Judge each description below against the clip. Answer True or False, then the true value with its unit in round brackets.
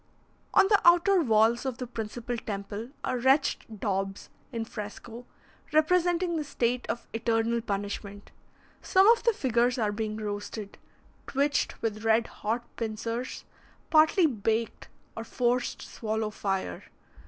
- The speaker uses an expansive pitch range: False (3.6 semitones)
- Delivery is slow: True (130 wpm)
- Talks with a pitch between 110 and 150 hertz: False (230 Hz)